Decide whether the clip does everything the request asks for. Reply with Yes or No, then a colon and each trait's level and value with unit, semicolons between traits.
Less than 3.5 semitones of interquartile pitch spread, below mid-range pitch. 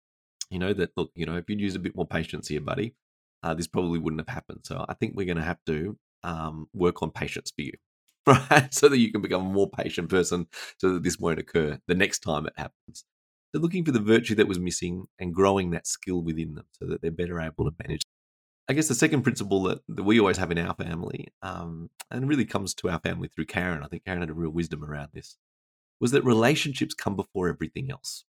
No: average, 4.1 semitones; very low, 90 Hz